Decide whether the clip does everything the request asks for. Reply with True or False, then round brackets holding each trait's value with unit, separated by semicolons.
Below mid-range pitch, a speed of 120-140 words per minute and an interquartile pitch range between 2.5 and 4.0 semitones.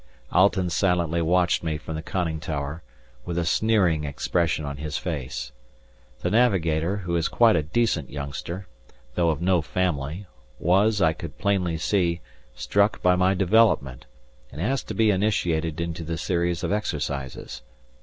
False (85 Hz; 155 wpm; 3.5 semitones)